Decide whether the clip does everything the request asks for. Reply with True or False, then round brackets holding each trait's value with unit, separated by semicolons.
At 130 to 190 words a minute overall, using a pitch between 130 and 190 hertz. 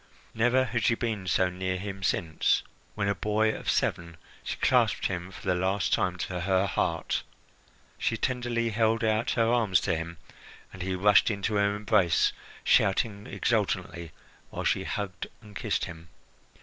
False (160 wpm; 100 Hz)